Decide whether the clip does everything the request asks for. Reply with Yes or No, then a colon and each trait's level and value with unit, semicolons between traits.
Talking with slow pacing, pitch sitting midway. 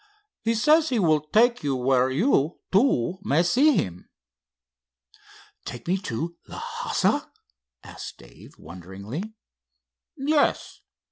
Yes: slow, 110 wpm; medium, 170 Hz